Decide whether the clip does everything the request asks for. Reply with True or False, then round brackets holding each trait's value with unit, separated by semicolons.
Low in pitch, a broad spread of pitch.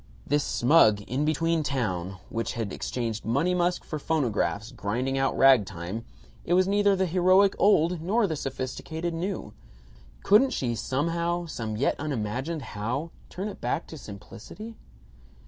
False (145 Hz; 7.2 semitones)